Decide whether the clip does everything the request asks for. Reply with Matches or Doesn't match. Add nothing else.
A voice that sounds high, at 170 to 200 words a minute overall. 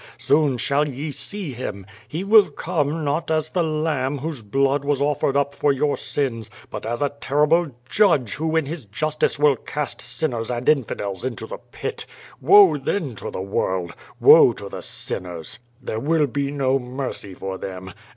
Doesn't match